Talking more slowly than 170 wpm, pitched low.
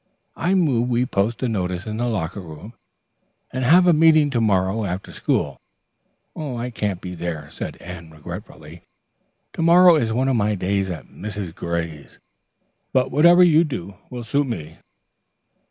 Yes: average, 160 wpm; low, 110 Hz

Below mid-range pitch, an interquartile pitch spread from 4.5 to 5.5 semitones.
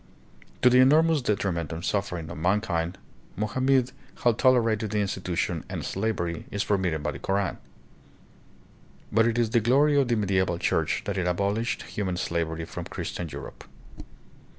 Yes: low, 100 Hz; average, 4.9 semitones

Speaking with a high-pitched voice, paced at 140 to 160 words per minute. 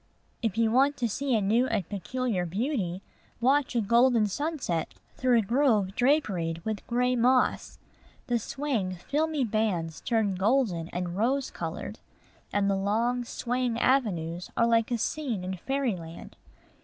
Yes: high, 230 Hz; average, 145 wpm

